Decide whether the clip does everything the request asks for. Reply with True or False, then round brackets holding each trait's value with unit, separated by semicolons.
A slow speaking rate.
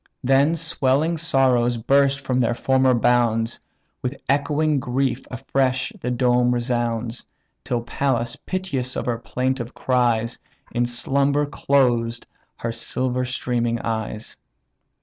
True (110 wpm)